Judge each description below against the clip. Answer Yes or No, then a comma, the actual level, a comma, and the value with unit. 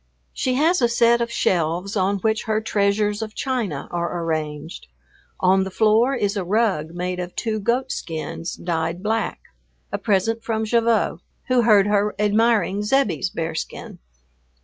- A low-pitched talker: No, high, 205 Hz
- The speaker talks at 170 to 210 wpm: No, average, 150 wpm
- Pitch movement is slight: No, average, 4.1 semitones